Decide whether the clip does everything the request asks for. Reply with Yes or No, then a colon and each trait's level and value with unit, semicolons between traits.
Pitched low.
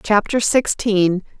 No: high, 205 Hz